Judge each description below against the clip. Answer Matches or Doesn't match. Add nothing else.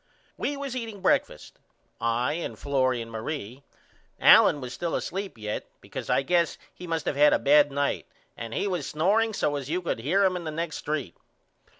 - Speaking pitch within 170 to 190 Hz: Doesn't match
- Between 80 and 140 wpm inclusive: Doesn't match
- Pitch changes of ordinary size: Doesn't match